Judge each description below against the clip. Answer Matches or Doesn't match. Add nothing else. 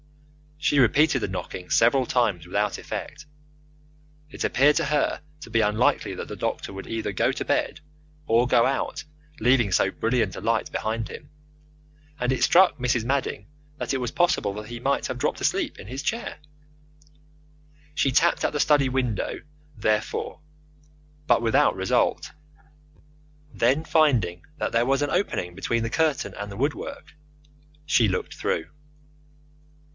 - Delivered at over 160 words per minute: Doesn't match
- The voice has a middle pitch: Doesn't match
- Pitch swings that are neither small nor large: Matches